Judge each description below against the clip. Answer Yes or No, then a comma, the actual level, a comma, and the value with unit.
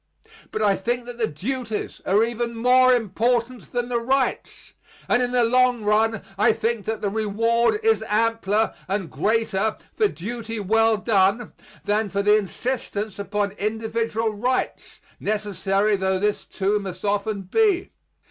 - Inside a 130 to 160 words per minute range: Yes, average, 150 wpm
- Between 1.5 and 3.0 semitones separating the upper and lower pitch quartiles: Yes, narrow, 2.6 semitones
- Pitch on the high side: Yes, high, 220 Hz